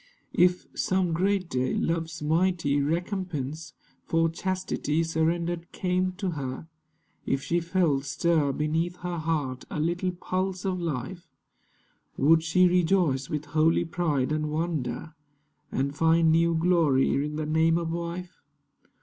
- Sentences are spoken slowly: Yes, slow, 130 wpm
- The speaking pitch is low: No, medium, 165 Hz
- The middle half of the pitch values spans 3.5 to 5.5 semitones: No, average, 2.7 semitones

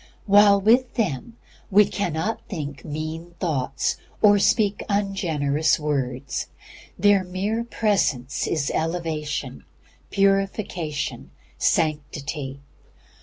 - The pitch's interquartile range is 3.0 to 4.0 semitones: No, wide, 5.5 semitones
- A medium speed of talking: No, slow, 85 wpm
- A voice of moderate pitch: Yes, medium, 170 Hz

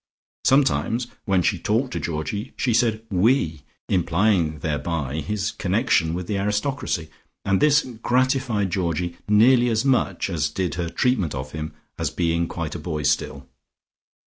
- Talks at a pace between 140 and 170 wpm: Yes, average, 145 wpm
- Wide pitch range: Yes, wide, 5.7 semitones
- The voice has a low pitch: Yes, very low, 95 Hz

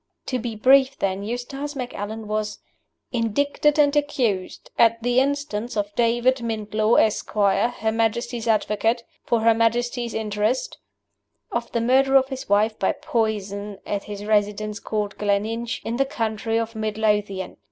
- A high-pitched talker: Yes, high, 225 Hz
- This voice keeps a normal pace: Yes, average, 145 wpm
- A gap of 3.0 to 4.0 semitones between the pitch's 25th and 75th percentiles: No, narrow, 2.6 semitones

